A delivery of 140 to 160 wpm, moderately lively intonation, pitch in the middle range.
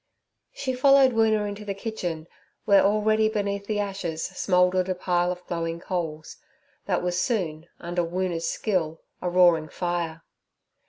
Yes: average, 145 wpm; average, 3.4 semitones; medium, 180 Hz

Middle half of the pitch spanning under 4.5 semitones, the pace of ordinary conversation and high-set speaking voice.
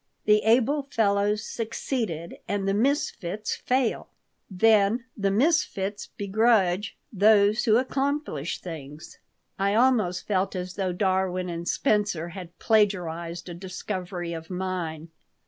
No: average, 3.8 semitones; slow, 115 wpm; high, 200 Hz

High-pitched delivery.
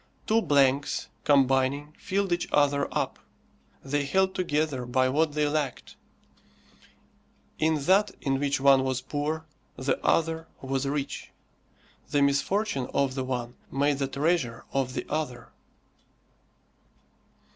No: medium, 140 Hz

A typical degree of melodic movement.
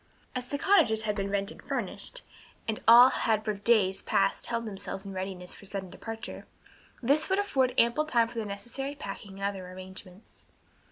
Yes: average, 3.8 semitones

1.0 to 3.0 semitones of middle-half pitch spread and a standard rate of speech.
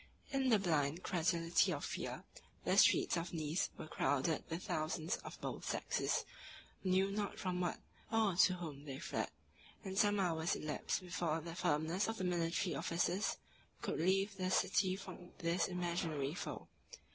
Yes: average, 2.7 semitones; average, 160 wpm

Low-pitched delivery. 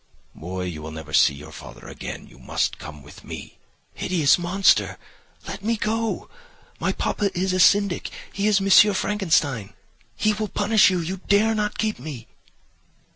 No: high, 190 Hz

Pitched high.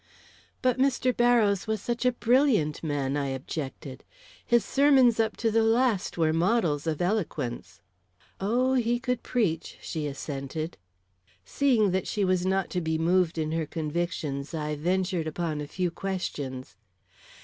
No: medium, 180 Hz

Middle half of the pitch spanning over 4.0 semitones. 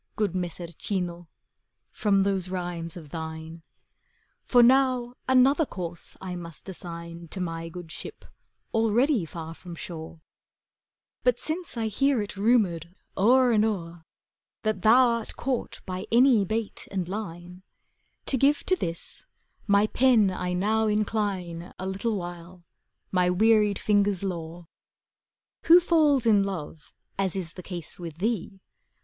Yes: average, 4.5 semitones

